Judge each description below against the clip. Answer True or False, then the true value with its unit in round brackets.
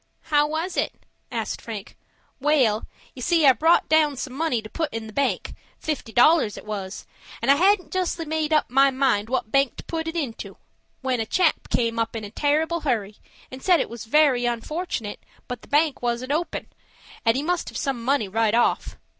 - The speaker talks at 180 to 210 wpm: True (200 wpm)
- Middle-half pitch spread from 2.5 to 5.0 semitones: False (5.4 semitones)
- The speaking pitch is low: False (270 Hz)